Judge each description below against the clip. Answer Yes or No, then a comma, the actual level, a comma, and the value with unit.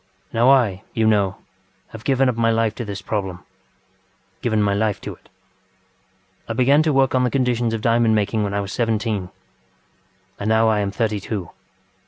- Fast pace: No, average, 180 wpm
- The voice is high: No, low, 110 Hz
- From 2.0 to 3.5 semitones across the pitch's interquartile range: Yes, average, 2.7 semitones